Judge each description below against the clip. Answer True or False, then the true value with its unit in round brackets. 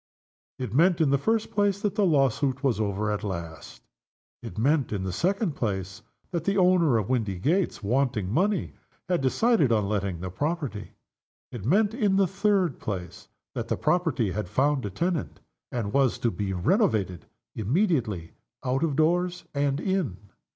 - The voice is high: False (135 Hz)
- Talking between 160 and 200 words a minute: True (165 wpm)